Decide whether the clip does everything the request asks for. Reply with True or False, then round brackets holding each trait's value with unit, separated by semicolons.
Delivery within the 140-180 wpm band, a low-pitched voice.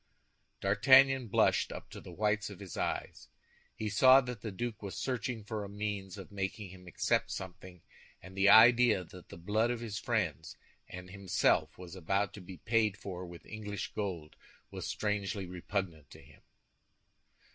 True (170 wpm; 100 Hz)